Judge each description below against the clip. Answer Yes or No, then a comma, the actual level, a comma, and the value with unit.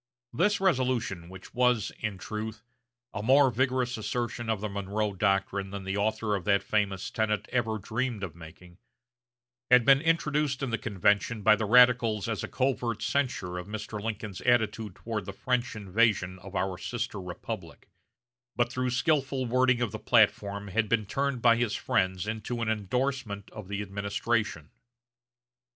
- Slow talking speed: No, average, 160 wpm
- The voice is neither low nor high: No, low, 110 Hz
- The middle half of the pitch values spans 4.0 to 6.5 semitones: No, average, 3.6 semitones